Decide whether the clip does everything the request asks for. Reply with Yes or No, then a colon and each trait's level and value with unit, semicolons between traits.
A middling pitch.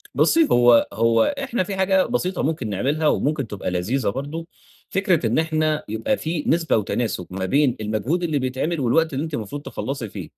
Yes: medium, 145 Hz